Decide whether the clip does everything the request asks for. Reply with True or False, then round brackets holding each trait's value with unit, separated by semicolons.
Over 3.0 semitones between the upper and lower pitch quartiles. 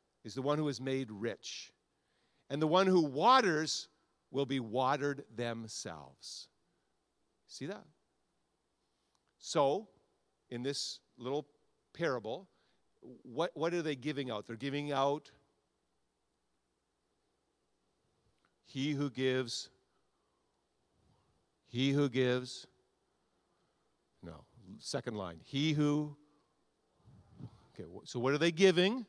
False (2.6 semitones)